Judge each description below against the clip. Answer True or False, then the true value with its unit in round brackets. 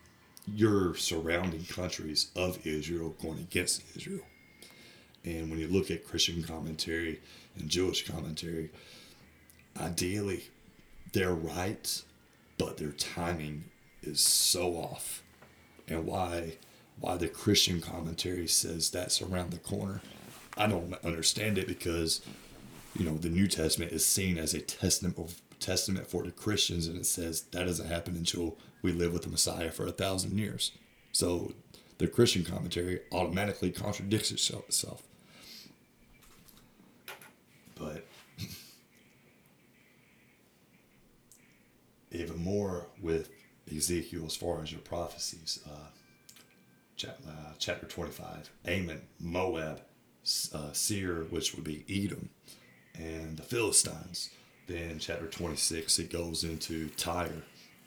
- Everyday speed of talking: False (115 wpm)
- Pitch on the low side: True (85 Hz)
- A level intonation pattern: True (2.0 semitones)